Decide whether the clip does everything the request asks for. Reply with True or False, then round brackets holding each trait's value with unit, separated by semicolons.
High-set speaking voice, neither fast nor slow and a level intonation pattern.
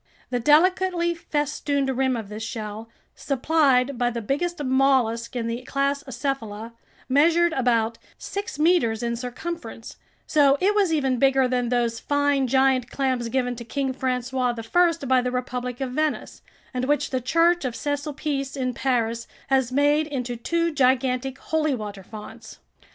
False (265 Hz; 155 wpm; 3.2 semitones)